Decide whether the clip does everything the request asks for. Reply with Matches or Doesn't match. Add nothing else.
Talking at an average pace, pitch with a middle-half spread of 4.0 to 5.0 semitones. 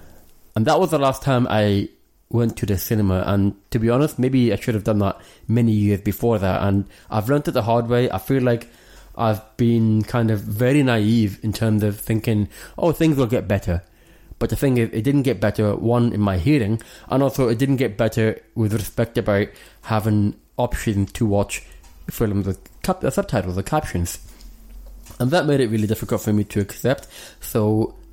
Doesn't match